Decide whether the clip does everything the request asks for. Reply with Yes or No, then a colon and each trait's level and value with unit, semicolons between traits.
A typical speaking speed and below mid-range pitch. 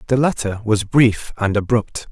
Yes: average, 170 wpm; low, 110 Hz